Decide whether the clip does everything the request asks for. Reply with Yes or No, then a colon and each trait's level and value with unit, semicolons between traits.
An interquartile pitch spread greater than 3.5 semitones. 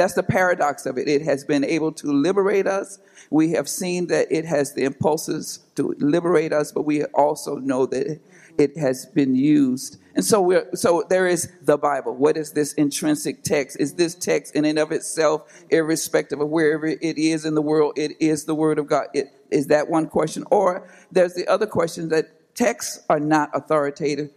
No: average, 2.9 semitones